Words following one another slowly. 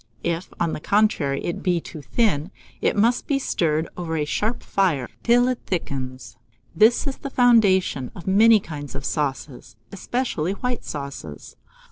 No: average, 155 wpm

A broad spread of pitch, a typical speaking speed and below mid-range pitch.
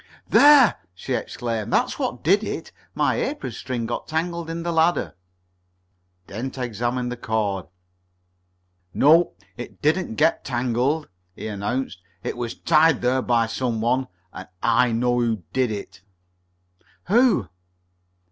No: wide, 5.7 semitones; slow, 130 wpm; low, 125 Hz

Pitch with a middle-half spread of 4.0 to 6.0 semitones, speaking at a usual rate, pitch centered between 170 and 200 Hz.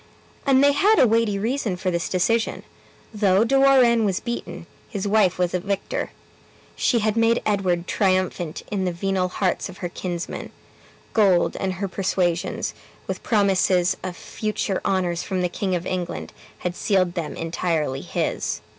No: average, 3.3 semitones; average, 160 wpm; high, 190 Hz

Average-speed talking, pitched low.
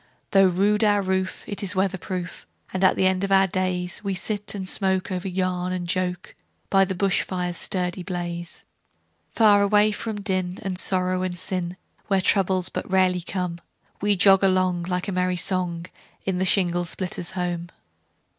No: average, 155 wpm; medium, 185 Hz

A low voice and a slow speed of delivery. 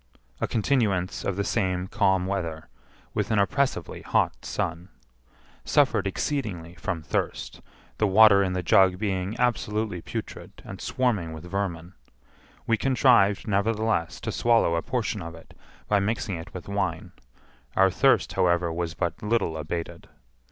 No: very low, 95 Hz; average, 145 wpm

